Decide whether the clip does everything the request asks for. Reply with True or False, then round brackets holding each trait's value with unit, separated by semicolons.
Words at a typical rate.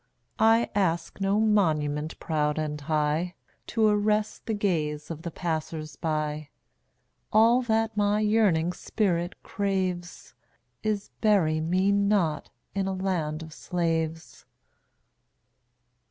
False (110 wpm)